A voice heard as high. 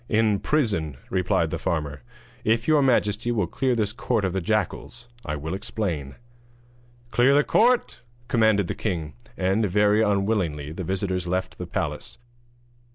No: low, 100 Hz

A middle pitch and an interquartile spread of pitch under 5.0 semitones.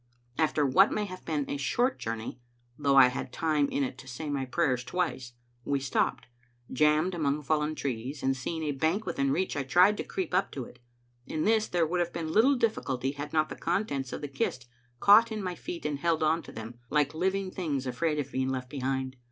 Yes: medium, 150 Hz; average, 4.6 semitones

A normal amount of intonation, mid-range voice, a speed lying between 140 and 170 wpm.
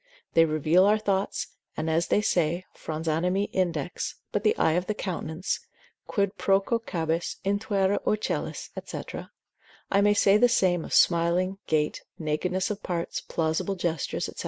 Yes: average, 3.6 semitones; medium, 180 Hz; average, 150 wpm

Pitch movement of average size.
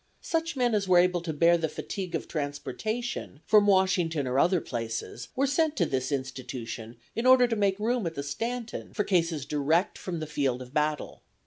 No: wide, 7.0 semitones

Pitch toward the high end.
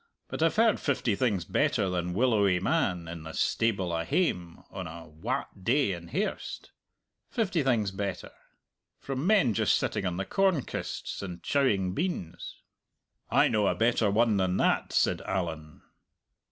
No: low, 100 Hz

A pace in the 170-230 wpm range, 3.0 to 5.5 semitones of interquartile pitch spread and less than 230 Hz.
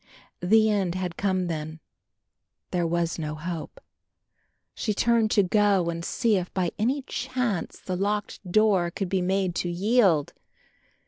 No: average, 145 wpm; average, 3.5 semitones; medium, 185 Hz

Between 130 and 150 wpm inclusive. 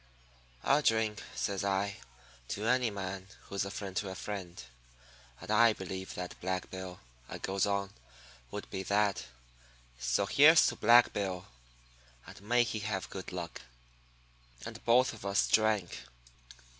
Yes: average, 145 wpm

